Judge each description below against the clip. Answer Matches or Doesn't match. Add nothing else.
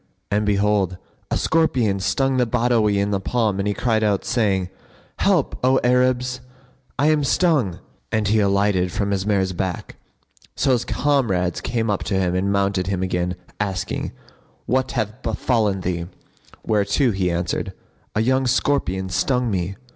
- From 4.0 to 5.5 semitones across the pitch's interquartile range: Matches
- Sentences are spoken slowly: Doesn't match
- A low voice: Matches